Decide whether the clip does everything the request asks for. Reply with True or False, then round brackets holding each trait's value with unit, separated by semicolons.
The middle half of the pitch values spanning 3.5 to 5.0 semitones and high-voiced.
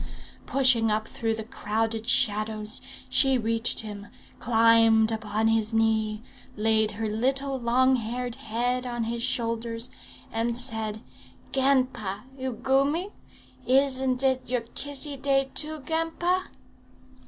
False (3.0 semitones; 235 Hz)